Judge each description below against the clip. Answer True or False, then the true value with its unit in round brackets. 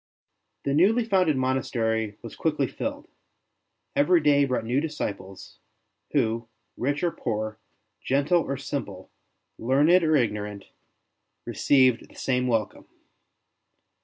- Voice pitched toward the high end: False (130 Hz)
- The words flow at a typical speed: False (110 wpm)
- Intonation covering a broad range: False (5.0 semitones)